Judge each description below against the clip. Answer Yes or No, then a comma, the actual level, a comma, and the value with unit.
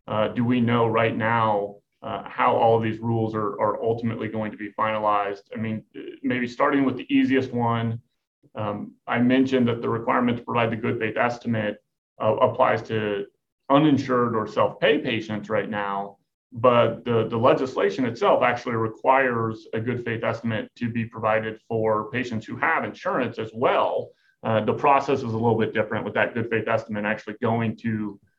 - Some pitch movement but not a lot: No, narrow, 2.1 semitones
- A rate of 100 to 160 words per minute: No, average, 180 wpm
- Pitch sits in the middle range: No, low, 115 Hz